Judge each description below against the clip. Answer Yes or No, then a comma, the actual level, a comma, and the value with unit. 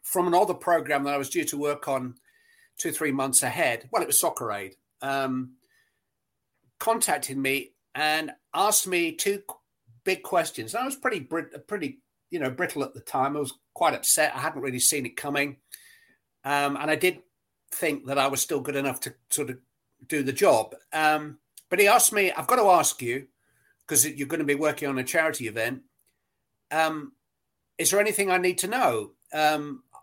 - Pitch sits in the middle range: Yes, medium, 145 Hz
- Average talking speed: Yes, average, 190 wpm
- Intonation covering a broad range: No, average, 4.1 semitones